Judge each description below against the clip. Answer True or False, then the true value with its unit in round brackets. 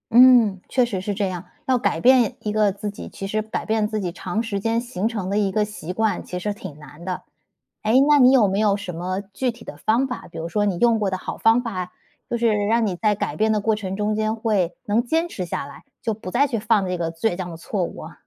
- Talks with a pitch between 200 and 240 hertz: True (210 Hz)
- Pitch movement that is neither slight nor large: True (3.3 semitones)